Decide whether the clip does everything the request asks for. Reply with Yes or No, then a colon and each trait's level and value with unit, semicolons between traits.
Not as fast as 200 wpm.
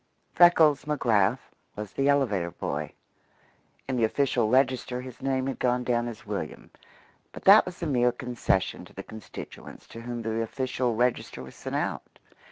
Yes: average, 165 wpm